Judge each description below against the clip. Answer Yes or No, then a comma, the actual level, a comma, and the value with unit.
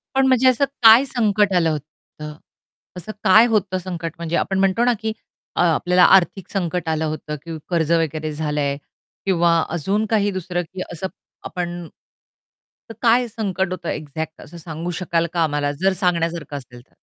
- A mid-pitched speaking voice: Yes, medium, 175 Hz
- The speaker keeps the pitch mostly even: No, average, 3.6 semitones